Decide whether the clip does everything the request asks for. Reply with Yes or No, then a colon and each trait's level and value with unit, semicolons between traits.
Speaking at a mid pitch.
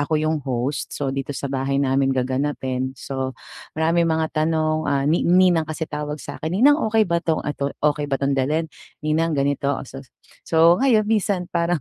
Yes: medium, 150 Hz